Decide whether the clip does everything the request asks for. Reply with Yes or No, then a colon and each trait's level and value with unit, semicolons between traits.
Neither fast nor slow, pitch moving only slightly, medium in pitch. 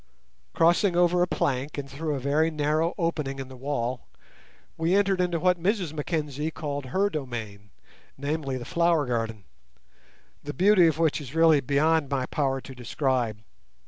No: average, 155 wpm; average, 3.9 semitones; medium, 150 Hz